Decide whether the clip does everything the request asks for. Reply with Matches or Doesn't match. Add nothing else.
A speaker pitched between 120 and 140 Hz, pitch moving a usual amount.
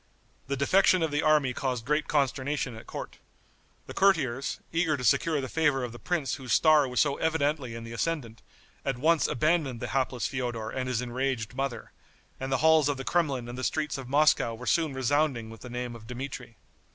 Matches